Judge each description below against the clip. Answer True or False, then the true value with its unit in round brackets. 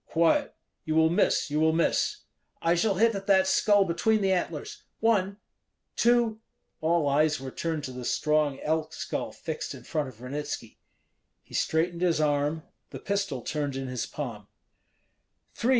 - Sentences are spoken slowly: False (165 wpm)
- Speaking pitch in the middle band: True (160 Hz)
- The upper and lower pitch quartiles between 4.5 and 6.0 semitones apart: True (4.8 semitones)